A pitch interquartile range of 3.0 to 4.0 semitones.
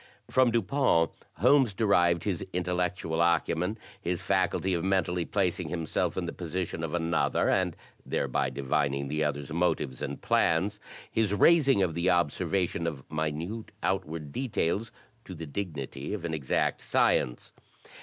Yes: average, 3.7 semitones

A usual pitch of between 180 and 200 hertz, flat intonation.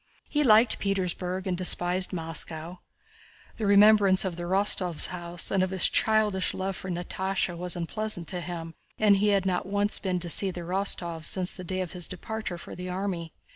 Yes: medium, 185 Hz; narrow, 2.1 semitones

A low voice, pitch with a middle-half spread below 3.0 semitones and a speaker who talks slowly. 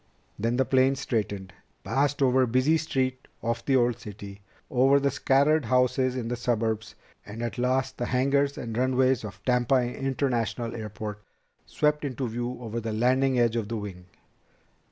No: low, 125 Hz; narrow, 2.6 semitones; average, 165 wpm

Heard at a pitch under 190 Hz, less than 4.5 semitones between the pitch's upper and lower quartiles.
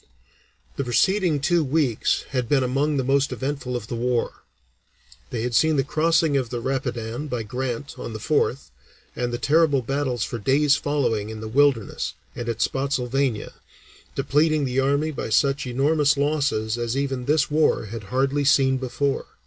Yes: low, 135 Hz; average, 3.1 semitones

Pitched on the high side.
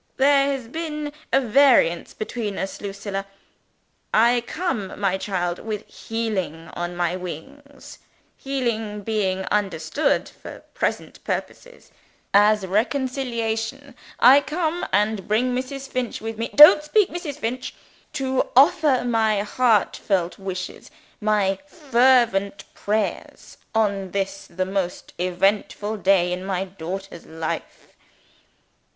Yes: high, 215 Hz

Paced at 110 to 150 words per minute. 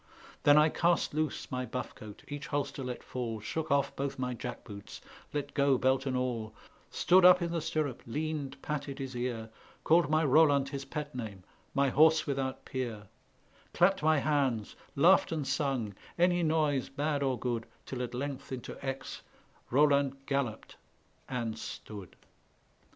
No: average, 160 wpm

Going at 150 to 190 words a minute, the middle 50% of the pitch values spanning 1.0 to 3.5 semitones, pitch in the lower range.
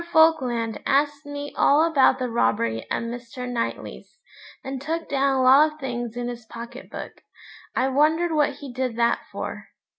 No: average, 170 wpm; average, 3.2 semitones; very high, 265 Hz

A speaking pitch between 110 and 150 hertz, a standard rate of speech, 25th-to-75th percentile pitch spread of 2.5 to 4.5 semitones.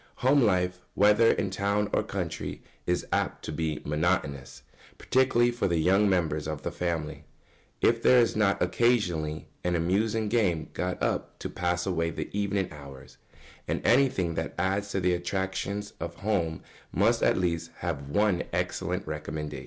No: very low, 90 Hz; average, 160 wpm; average, 4.0 semitones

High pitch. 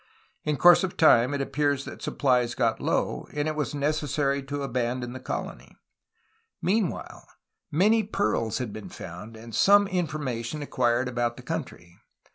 No: medium, 140 Hz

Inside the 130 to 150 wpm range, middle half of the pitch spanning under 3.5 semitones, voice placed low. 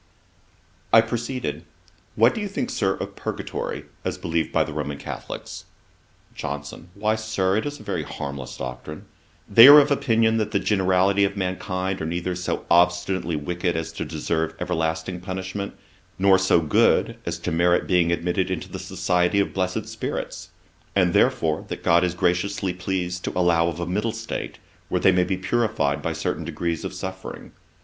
No: average, 170 wpm; average, 2.7 semitones; very low, 90 Hz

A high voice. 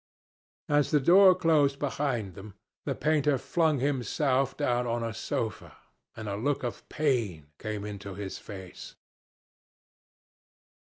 No: low, 125 Hz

